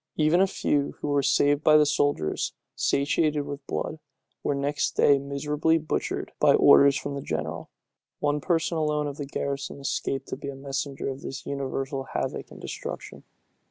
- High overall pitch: No, medium, 145 Hz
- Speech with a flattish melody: Yes, narrow, 1.4 semitones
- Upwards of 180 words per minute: No, average, 170 wpm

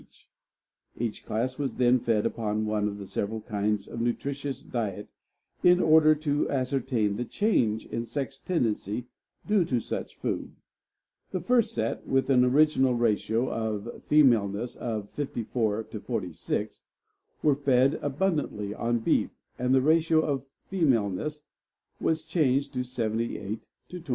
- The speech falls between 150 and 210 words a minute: No, slow, 135 wpm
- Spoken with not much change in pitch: No, average, 4.9 semitones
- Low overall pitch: Yes, low, 125 Hz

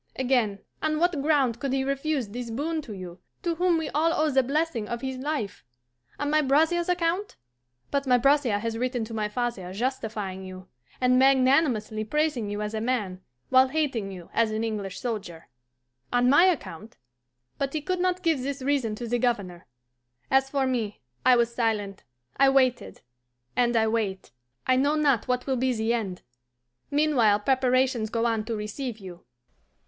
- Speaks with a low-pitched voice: No, very high, 250 Hz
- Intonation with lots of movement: No, average, 4.4 semitones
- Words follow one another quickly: No, average, 175 wpm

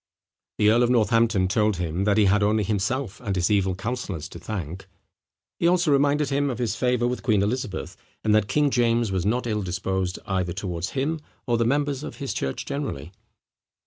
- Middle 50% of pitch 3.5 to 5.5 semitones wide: Yes, average, 4.8 semitones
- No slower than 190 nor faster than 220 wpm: Yes, average, 195 wpm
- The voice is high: No, low, 110 Hz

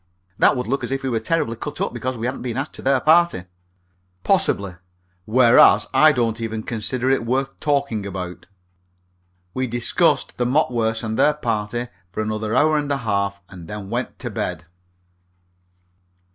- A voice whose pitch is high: No, low, 115 Hz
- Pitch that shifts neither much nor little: Yes, average, 3.8 semitones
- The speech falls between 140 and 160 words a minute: No, average, 170 wpm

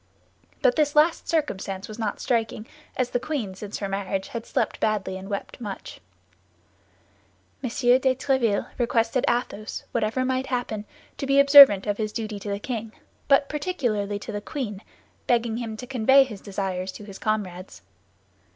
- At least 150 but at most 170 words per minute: Yes, average, 160 wpm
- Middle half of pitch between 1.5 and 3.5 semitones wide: No, average, 4.3 semitones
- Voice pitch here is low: No, high, 225 Hz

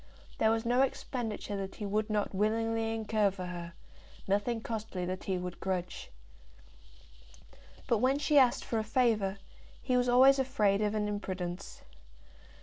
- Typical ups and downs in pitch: Yes, average, 3.5 semitones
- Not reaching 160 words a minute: Yes, average, 150 wpm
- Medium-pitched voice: No, high, 215 Hz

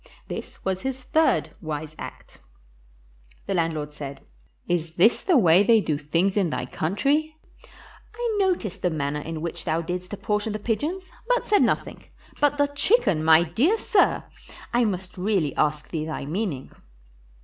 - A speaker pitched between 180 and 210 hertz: Yes, medium, 185 Hz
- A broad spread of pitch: Yes, wide, 9.0 semitones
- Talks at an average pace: Yes, average, 160 wpm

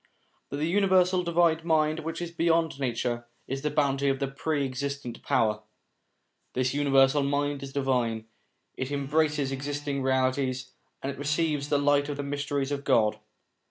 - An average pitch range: No, narrow, 2.1 semitones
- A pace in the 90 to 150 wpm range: No, average, 160 wpm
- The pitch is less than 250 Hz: Yes, medium, 140 Hz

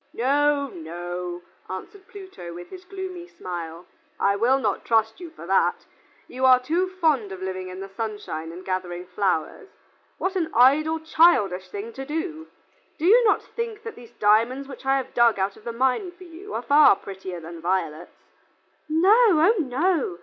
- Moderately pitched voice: No, very high, 250 Hz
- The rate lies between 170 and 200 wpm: Yes, average, 180 wpm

